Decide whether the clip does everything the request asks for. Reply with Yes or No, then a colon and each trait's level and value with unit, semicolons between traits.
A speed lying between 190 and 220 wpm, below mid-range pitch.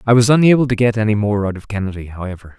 No: fast, 255 wpm; low, 110 Hz